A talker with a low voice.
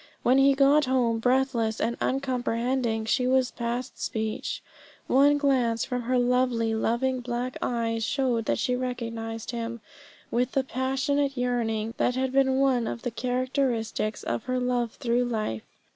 No: high, 245 Hz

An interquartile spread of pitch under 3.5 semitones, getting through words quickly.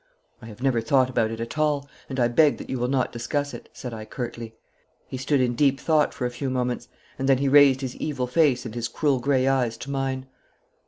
Yes: narrow, 2.4 semitones; fast, 235 wpm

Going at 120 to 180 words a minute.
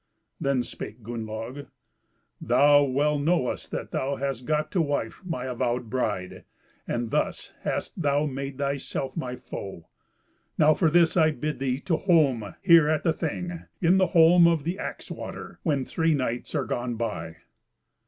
Yes: average, 160 wpm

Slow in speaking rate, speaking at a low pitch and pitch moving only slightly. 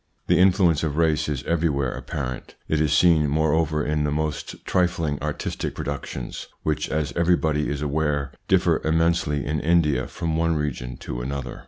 No: average, 160 wpm; very low, 75 Hz; narrow, 2.3 semitones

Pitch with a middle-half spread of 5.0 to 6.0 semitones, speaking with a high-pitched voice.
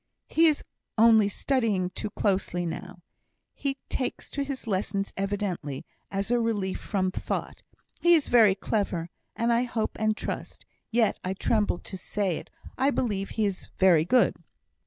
No: average, 3.7 semitones; high, 205 Hz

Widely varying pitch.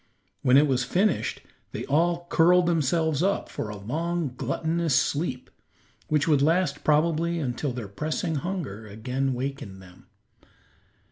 No: average, 5.0 semitones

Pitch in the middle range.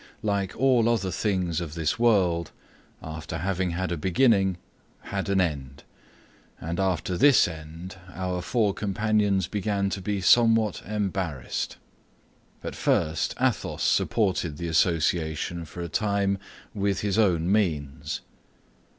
No: very low, 95 Hz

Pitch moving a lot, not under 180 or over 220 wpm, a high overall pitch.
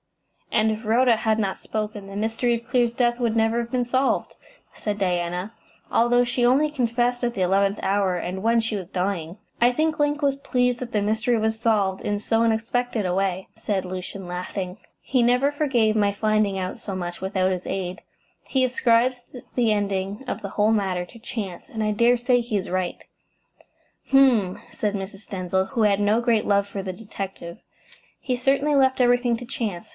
No: average, 3.9 semitones; average, 190 wpm; high, 220 Hz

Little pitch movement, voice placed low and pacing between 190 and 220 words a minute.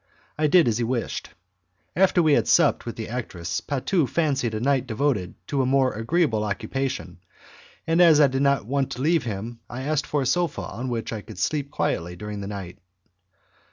No: average, 4.9 semitones; low, 130 Hz; average, 195 wpm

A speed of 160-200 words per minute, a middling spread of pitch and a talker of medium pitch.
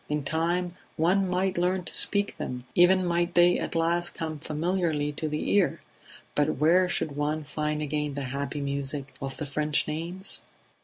Yes: average, 170 wpm; average, 3.2 semitones; medium, 160 Hz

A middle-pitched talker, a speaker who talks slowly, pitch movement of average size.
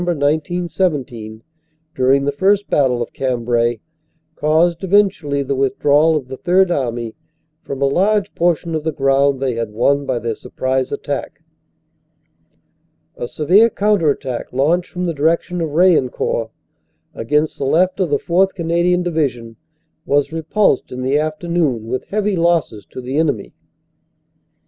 No: medium, 150 Hz; average, 145 wpm; average, 5.0 semitones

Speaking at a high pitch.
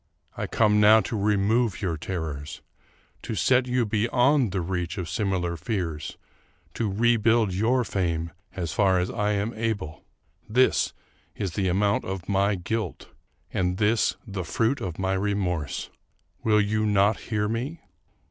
No: low, 100 Hz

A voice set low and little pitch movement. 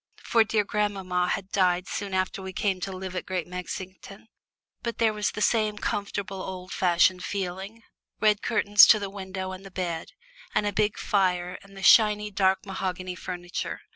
No: high, 190 Hz; narrow, 2.0 semitones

